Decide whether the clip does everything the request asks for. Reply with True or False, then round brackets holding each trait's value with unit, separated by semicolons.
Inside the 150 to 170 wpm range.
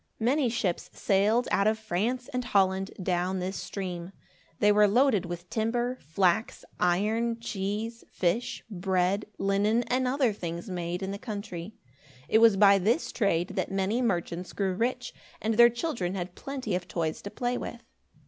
True (160 wpm)